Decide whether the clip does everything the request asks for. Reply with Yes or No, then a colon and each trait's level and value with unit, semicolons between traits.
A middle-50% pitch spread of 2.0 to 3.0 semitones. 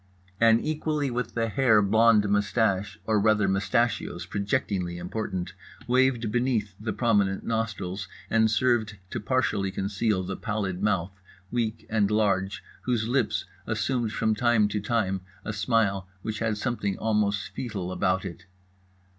Yes: average, 2.7 semitones